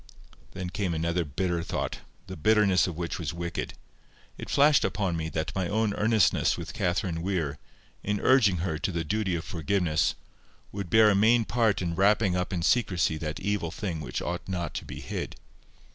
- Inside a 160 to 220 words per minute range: Yes, average, 185 wpm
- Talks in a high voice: No, very low, 90 Hz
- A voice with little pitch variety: No, average, 3.6 semitones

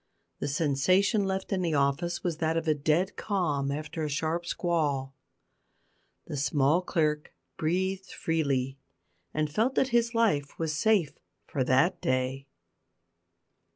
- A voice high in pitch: No, medium, 160 Hz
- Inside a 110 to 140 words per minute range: Yes, slow, 135 wpm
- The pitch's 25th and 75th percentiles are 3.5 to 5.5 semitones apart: Yes, average, 4.5 semitones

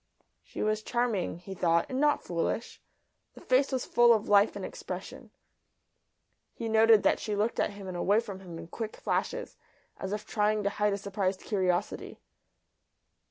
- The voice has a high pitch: Yes, high, 210 Hz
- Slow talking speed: No, average, 170 wpm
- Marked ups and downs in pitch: No, average, 3.0 semitones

